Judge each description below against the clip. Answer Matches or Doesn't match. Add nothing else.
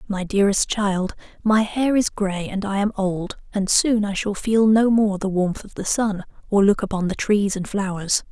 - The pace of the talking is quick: Matches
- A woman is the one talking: Matches